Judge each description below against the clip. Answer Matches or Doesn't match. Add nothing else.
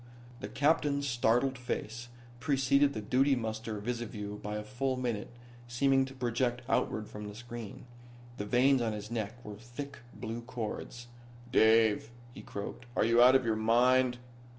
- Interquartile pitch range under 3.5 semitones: Matches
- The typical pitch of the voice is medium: Doesn't match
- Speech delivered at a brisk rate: Doesn't match